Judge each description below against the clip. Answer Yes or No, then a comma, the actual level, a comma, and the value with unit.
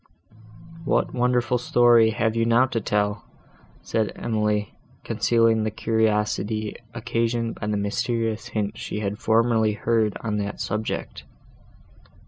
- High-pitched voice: No, low, 110 Hz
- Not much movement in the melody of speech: Yes, narrow, 1.7 semitones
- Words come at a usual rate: No, slow, 120 wpm